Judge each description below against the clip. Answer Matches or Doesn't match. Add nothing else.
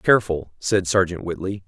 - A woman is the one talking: Doesn't match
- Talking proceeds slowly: Doesn't match